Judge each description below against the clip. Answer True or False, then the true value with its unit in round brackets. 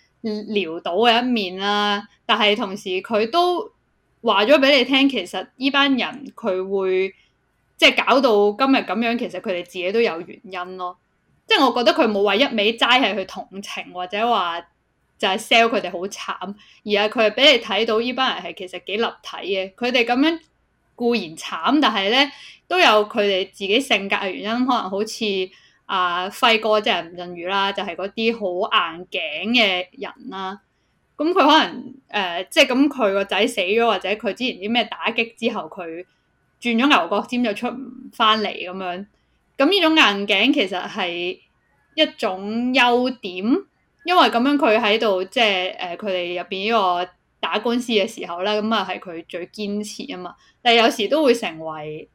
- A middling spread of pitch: True (4.4 semitones)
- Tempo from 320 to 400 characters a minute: False (255 characters per minute)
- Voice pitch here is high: True (215 Hz)